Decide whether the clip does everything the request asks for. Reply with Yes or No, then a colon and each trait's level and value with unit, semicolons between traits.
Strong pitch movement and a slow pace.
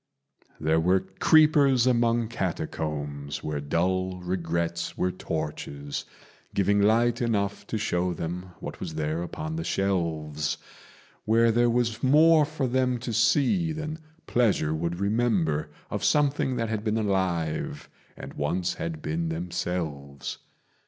Yes: wide, 6.6 semitones; slow, 130 wpm